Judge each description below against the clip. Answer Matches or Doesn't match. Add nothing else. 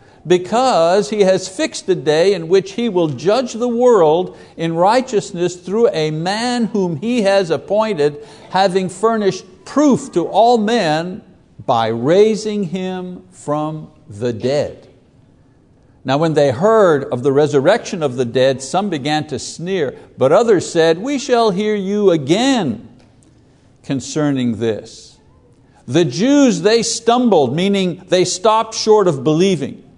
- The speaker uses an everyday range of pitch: Doesn't match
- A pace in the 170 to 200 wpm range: Doesn't match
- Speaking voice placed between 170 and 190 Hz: Matches